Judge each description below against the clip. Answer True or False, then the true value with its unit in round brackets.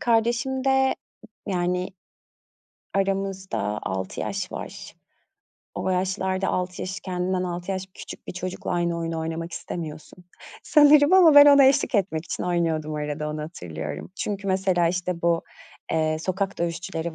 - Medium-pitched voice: True (180 Hz)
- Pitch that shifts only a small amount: False (3.0 semitones)